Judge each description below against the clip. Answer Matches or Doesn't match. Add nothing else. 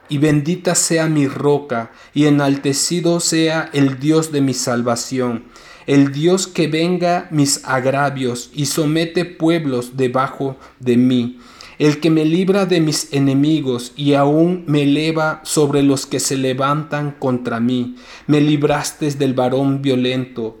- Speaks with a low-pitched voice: Doesn't match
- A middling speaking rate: Matches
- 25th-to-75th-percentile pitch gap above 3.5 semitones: Doesn't match